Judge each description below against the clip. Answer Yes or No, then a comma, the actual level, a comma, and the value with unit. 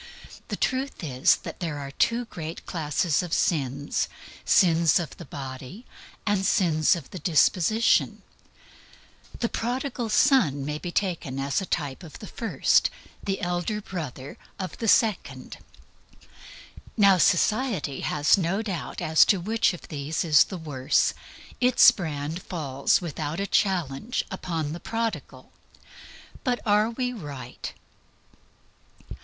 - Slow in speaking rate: Yes, slow, 130 wpm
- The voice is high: No, medium, 175 Hz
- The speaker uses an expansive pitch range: Yes, wide, 6.1 semitones